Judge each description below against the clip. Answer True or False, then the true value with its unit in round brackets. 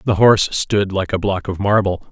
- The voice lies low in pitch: True (100 Hz)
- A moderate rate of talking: False (225 wpm)